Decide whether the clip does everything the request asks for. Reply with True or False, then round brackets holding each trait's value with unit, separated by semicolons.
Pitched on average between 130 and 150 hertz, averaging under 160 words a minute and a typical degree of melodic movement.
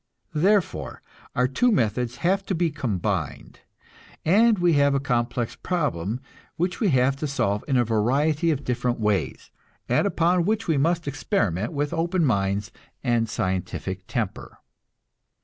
False (135 Hz; 145 wpm; 7.1 semitones)